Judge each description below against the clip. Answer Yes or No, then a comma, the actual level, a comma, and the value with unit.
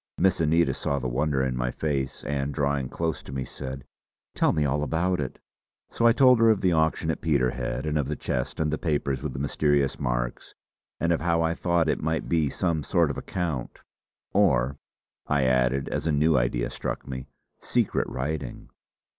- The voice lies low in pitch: Yes, very low, 75 Hz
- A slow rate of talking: No, average, 195 wpm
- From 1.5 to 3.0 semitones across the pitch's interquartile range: No, average, 3.6 semitones